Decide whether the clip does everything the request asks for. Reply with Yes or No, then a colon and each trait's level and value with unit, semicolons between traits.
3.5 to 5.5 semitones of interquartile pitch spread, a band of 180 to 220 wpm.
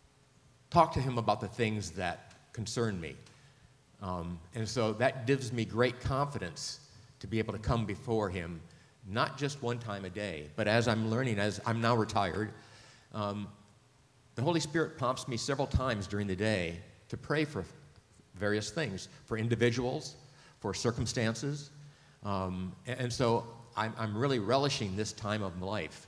No: average, 4.0 semitones; average, 165 wpm